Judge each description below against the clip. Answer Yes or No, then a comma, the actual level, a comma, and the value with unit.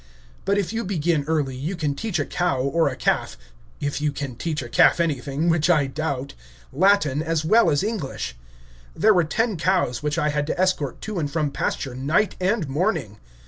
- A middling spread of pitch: Yes, average, 4.5 semitones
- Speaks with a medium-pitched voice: Yes, medium, 155 Hz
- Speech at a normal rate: Yes, average, 195 wpm